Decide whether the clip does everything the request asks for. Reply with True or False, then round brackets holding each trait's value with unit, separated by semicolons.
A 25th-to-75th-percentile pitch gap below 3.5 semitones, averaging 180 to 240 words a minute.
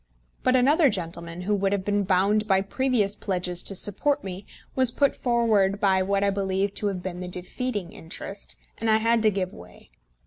True (2.9 semitones; 195 wpm)